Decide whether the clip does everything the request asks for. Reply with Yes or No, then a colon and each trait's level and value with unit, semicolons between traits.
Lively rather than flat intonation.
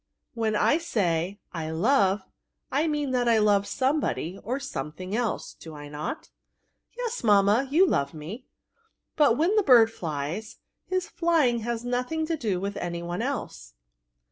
Yes: wide, 7.9 semitones